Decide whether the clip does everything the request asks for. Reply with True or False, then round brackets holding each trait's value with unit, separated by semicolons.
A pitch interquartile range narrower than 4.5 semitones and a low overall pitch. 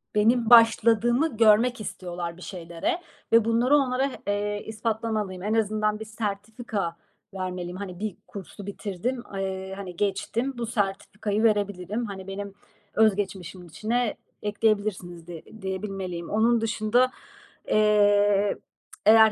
False (2.8 semitones; 210 Hz)